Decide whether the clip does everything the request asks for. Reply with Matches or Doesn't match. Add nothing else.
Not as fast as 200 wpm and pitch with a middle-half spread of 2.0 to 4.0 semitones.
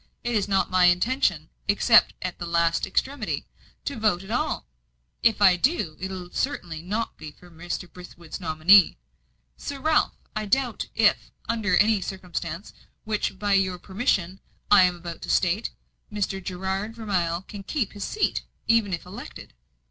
Matches